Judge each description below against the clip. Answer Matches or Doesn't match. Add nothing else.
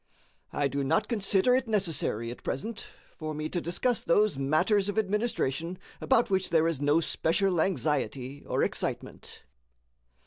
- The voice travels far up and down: Matches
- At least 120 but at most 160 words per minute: Matches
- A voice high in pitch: Doesn't match